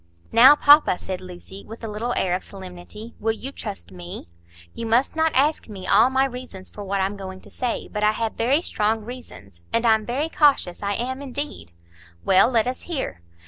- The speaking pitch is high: Yes, high, 225 Hz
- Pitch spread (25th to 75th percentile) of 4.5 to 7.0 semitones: Yes, average, 5.2 semitones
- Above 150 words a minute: Yes, average, 200 wpm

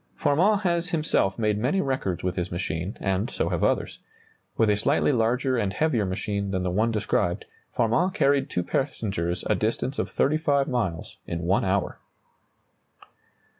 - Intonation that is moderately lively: No, wide, 6.7 semitones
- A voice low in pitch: Yes, low, 110 Hz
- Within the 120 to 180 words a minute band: Yes, average, 165 wpm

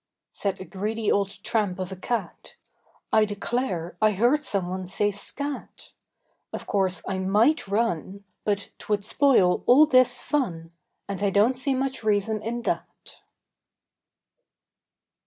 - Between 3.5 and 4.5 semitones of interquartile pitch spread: Yes, average, 4.1 semitones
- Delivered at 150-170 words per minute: No, slow, 135 wpm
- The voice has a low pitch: No, high, 205 Hz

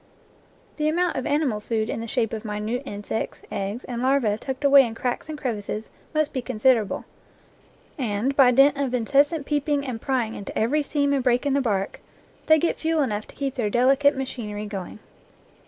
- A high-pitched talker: Yes, very high, 255 Hz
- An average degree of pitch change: Yes, average, 4.3 semitones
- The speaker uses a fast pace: No, average, 190 wpm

